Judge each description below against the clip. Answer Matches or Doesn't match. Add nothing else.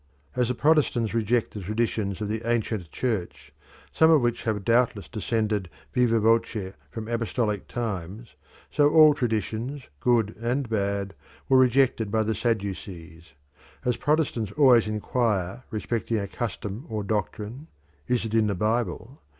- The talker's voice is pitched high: Doesn't match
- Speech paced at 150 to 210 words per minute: Doesn't match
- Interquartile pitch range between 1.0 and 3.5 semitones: Matches